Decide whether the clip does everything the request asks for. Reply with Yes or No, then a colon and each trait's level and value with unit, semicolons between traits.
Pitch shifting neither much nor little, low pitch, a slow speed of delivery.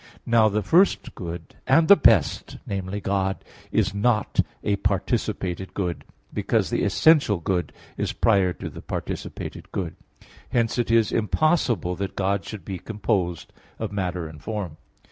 No: average, 3.6 semitones; low, 100 Hz; average, 145 wpm